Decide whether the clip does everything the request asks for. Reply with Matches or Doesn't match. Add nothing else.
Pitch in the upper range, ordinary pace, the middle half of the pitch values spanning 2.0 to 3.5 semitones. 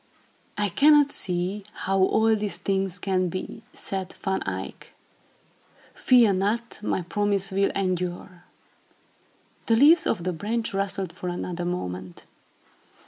Doesn't match